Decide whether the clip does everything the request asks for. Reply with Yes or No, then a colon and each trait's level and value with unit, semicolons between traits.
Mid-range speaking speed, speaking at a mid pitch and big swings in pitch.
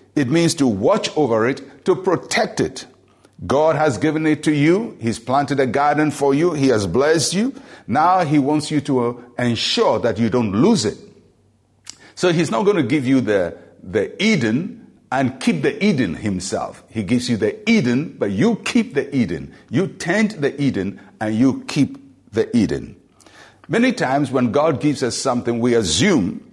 Yes: average, 180 wpm; medium, 145 Hz; wide, 5.7 semitones